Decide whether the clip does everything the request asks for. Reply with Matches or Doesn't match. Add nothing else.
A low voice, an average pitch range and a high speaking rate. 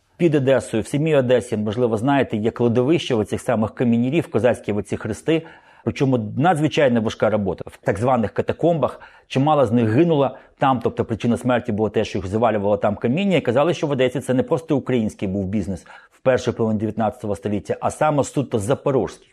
Matches